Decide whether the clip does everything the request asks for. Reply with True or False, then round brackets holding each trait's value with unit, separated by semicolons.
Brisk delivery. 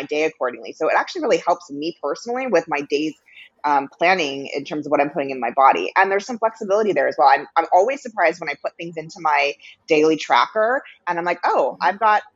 True (235 wpm)